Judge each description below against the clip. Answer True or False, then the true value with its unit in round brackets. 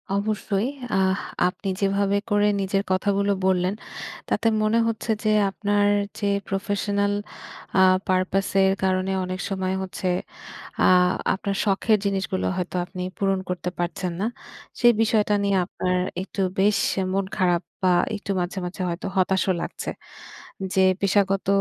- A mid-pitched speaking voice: False (195 Hz)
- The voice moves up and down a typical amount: False (1.5 semitones)